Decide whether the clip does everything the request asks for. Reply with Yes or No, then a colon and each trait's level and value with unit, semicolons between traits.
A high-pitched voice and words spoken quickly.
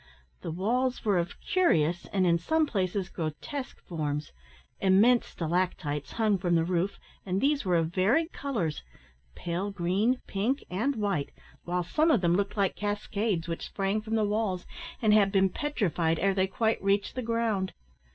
No: high, 195 Hz; average, 165 wpm